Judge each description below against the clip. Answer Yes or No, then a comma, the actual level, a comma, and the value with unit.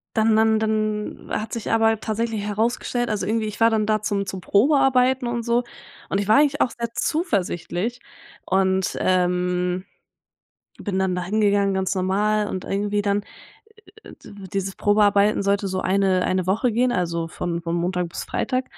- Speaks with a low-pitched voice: No, high, 205 Hz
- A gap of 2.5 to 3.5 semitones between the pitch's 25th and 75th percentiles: Yes, average, 3.0 semitones